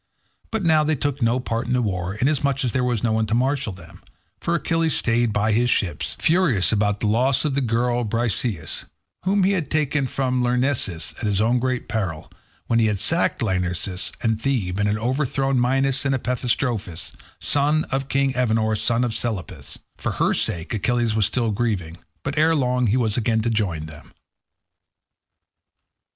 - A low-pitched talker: Yes, low, 120 Hz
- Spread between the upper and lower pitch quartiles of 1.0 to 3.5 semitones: No, average, 4.1 semitones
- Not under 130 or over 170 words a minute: No, average, 180 wpm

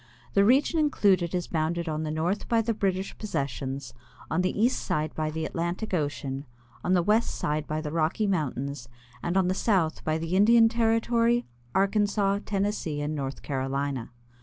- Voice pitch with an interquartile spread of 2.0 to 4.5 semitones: No, average, 5.2 semitones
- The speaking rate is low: No, average, 160 wpm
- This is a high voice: No, medium, 175 Hz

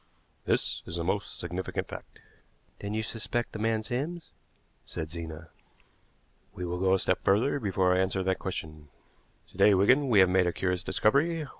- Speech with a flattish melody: No, average, 3.9 semitones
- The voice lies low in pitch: Yes, very low, 95 Hz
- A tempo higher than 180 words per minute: No, average, 175 wpm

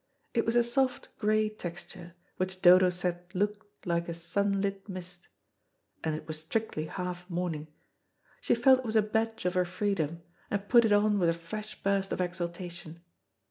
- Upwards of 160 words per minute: Yes, average, 175 wpm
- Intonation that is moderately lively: Yes, average, 3.4 semitones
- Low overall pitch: No, medium, 185 Hz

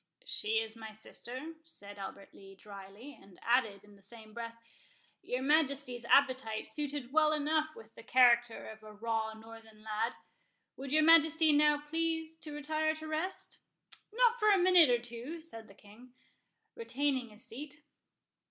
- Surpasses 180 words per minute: No, average, 155 wpm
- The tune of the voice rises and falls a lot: Yes, wide, 5.9 semitones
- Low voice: No, very high, 255 Hz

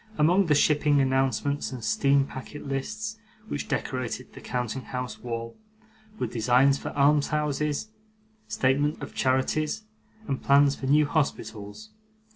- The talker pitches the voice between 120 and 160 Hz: Yes, medium, 140 Hz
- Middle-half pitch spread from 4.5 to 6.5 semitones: No, average, 2.7 semitones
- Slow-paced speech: Yes, slow, 125 wpm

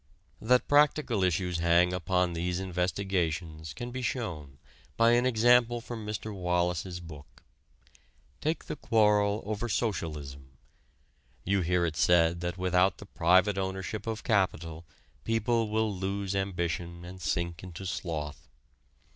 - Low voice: Yes, very low, 95 Hz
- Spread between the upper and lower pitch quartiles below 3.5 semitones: No, average, 3.9 semitones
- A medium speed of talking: No, slow, 130 wpm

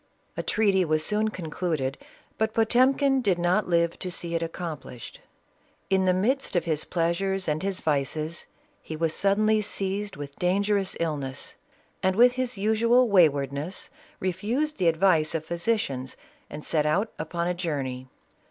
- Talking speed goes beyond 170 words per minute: No, average, 150 wpm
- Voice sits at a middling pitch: Yes, medium, 180 Hz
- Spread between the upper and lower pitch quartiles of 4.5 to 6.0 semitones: Yes, average, 4.9 semitones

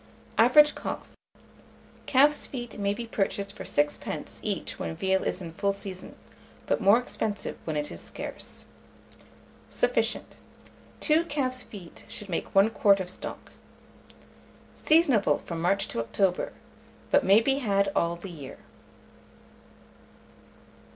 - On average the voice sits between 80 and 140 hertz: No, high, 200 Hz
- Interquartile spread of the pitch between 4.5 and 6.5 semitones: Yes, average, 5.2 semitones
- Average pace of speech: No, slow, 130 wpm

